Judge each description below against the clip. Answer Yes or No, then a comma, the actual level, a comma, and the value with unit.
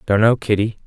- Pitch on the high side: No, low, 105 Hz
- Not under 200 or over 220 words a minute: Yes, fast, 210 wpm